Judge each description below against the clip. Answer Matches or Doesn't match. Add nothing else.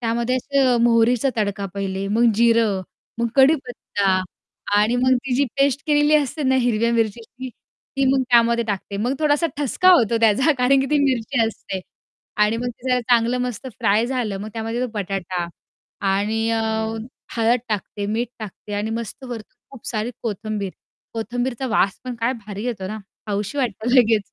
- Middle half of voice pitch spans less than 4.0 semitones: Matches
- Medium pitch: Doesn't match